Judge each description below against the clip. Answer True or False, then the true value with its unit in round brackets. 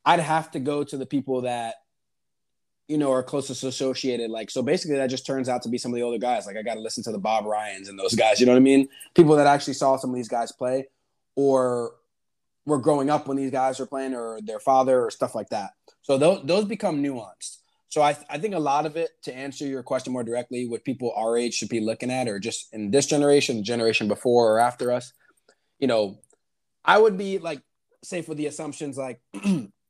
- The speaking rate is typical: False (235 wpm)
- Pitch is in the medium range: False (130 Hz)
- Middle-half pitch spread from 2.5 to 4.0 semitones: True (3.0 semitones)